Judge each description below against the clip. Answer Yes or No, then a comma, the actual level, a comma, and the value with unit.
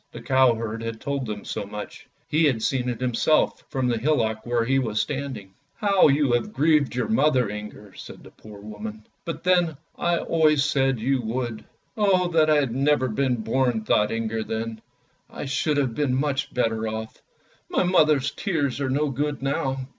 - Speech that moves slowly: No, average, 200 wpm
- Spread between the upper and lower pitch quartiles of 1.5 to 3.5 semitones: No, average, 4.8 semitones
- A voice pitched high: No, low, 130 Hz